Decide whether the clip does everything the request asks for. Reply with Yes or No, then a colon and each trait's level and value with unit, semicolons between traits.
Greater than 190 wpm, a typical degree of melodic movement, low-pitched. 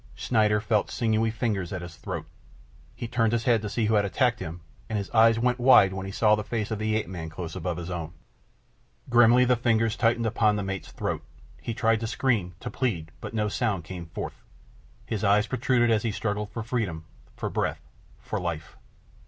Yes: fast, 205 wpm; average, 3.4 semitones; low, 110 Hz